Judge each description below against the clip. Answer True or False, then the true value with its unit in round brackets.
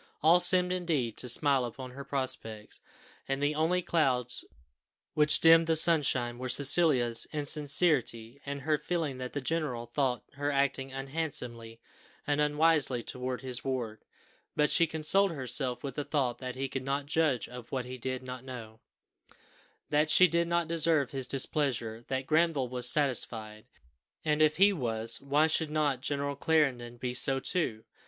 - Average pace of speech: True (160 wpm)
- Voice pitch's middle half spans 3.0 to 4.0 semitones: True (3.7 semitones)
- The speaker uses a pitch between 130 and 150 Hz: True (140 Hz)